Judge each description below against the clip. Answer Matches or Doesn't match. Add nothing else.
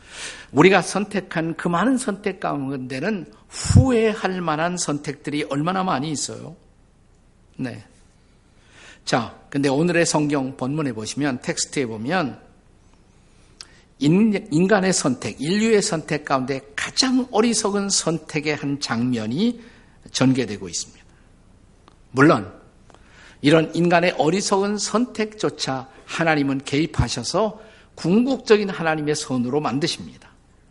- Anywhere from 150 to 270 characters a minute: Matches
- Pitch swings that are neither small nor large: Doesn't match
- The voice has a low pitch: Doesn't match